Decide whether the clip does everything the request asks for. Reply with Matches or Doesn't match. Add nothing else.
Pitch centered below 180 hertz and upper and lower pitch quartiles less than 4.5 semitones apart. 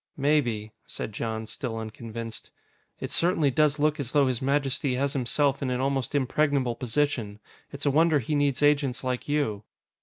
Matches